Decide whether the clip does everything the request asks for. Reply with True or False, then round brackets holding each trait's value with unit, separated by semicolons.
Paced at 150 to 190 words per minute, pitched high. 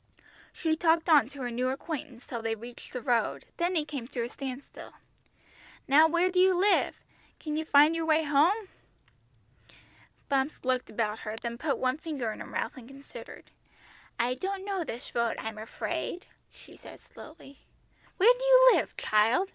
True (175 wpm; 285 Hz)